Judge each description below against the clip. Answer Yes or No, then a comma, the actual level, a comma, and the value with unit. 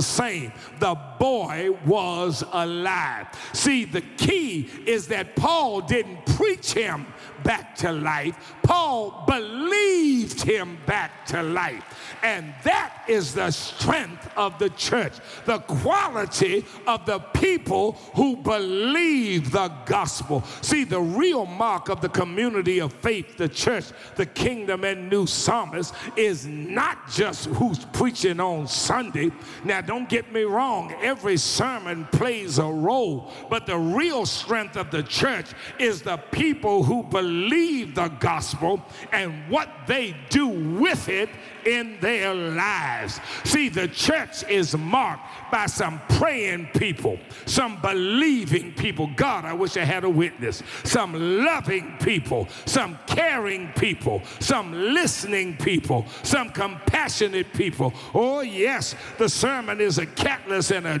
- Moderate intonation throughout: No, wide, 5.7 semitones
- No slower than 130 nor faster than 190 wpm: Yes, slow, 135 wpm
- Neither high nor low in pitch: No, high, 195 Hz